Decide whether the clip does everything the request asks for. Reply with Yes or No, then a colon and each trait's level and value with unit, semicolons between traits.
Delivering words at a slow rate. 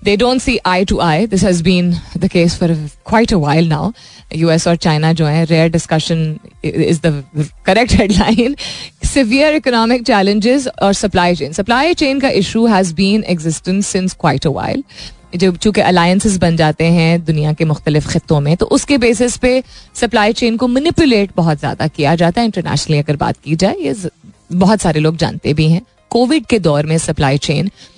No: average, 180 wpm